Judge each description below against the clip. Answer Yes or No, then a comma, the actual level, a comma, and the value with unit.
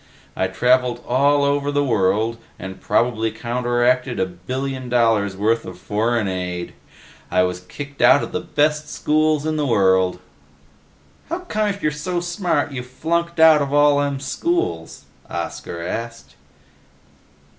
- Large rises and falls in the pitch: Yes, wide, 6.1 semitones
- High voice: No, low, 125 Hz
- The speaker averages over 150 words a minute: No, average, 145 wpm